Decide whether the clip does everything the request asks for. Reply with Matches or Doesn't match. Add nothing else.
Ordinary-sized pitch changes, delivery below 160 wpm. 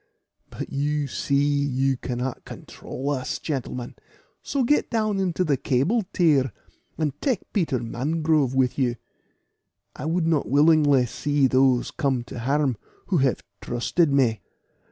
Matches